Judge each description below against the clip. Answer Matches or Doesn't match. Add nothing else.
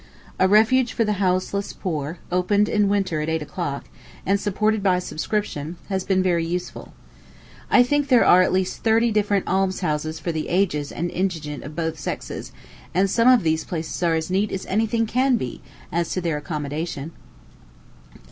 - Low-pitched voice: Doesn't match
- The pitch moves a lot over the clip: Doesn't match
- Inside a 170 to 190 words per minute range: Matches